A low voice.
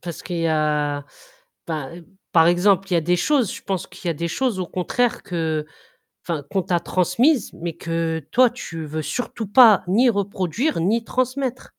No: medium, 180 Hz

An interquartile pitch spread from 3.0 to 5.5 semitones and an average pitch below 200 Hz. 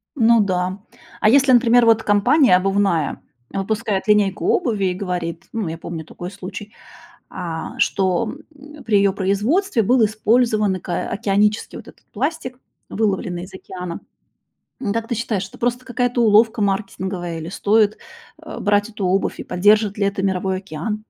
No: average, 3.3 semitones; high, 205 Hz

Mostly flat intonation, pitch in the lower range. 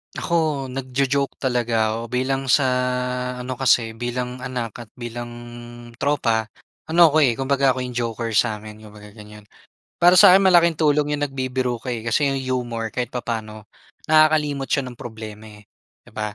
No: average, 3.6 semitones; low, 125 Hz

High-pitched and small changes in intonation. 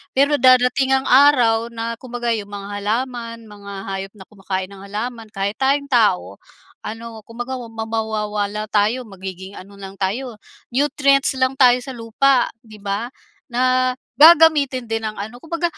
No: high, 230 Hz; average, 3.8 semitones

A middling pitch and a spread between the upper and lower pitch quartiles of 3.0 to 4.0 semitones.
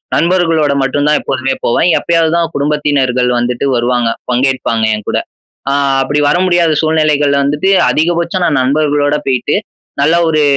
Yes: medium, 145 Hz; average, 3.5 semitones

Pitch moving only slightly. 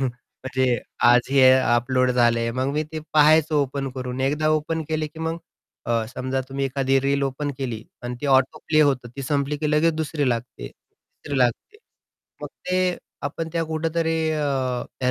No: average, 3.2 semitones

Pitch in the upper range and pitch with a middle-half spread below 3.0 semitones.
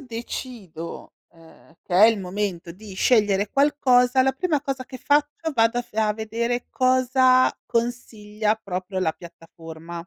No: high, 225 Hz; wide, 5.4 semitones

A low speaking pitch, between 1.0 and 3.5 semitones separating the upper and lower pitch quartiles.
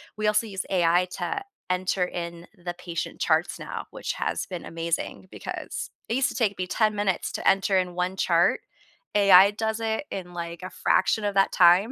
No: medium, 185 Hz; average, 2.9 semitones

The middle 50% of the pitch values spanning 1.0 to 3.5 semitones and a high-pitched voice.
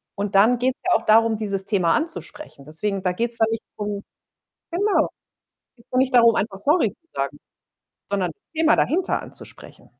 No: average, 4.9 semitones; high, 220 Hz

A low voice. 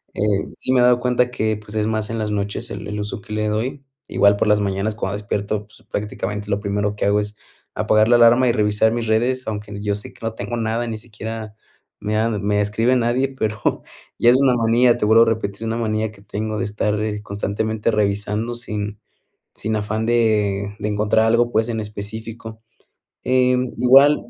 Yes: low, 110 Hz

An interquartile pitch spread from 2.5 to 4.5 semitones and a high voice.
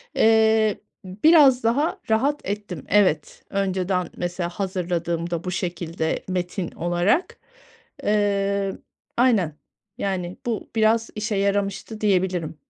Yes: average, 3.6 semitones; high, 195 Hz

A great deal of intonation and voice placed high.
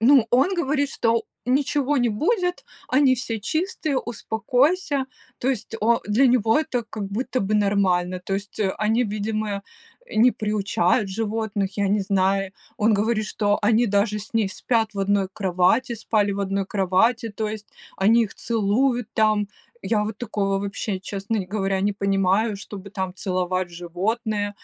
No: average, 3.0 semitones; high, 210 Hz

